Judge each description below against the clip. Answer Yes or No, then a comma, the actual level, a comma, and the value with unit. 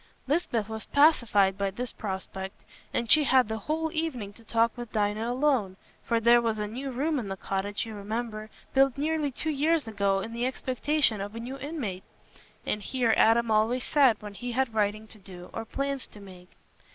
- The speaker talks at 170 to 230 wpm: Yes, average, 195 wpm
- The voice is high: Yes, high, 230 Hz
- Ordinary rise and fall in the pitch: Yes, average, 4.4 semitones